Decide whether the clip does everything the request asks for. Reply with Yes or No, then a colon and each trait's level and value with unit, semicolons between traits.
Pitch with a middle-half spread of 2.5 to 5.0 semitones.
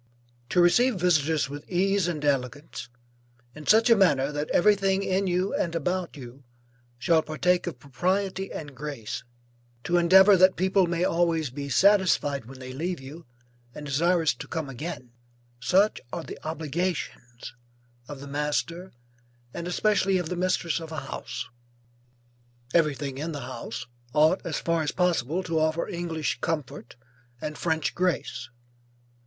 Yes: average, 4.2 semitones